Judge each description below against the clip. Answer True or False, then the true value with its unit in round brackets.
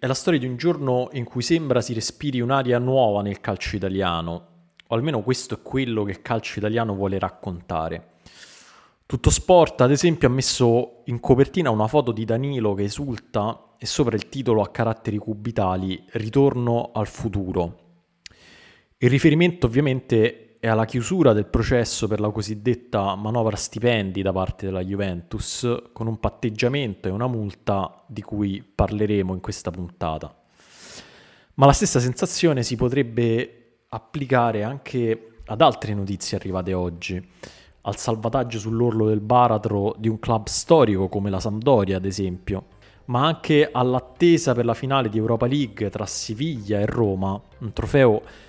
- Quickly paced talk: False (150 wpm)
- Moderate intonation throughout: True (4.0 semitones)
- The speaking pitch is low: True (115 Hz)